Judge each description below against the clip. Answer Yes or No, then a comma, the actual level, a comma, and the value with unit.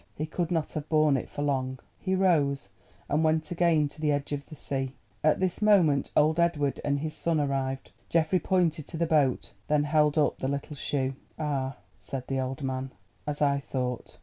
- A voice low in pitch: No, medium, 150 Hz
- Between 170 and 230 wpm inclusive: Yes, average, 200 wpm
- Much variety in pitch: No, narrow, 2.6 semitones